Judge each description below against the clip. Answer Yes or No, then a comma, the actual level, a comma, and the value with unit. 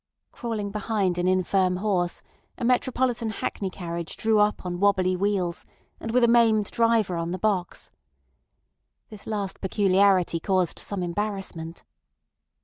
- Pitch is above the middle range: Yes, high, 195 Hz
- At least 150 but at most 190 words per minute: No, slow, 135 wpm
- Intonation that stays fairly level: No, average, 3.1 semitones